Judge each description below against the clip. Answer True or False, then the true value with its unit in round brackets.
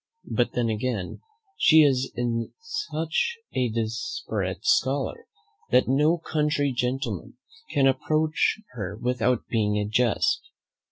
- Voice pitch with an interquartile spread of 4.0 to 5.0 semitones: True (4.7 semitones)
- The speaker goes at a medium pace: False (110 wpm)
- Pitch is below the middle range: True (130 Hz)